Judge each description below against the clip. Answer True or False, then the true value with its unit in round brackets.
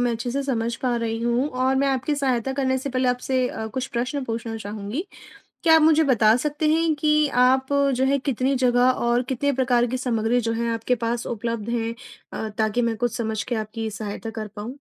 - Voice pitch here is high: True (245 Hz)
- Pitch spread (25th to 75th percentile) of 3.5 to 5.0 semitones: False (2.7 semitones)